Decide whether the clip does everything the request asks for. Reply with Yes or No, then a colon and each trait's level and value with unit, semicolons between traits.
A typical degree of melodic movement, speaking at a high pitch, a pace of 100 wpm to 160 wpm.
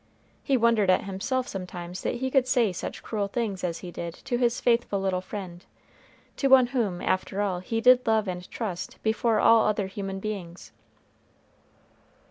No: average, 4.3 semitones; high, 205 Hz; average, 170 wpm